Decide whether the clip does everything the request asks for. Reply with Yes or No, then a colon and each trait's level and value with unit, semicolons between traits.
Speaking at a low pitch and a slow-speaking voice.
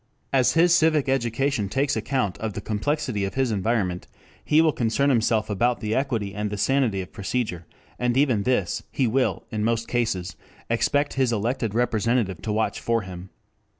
No: low, 115 Hz; average, 175 wpm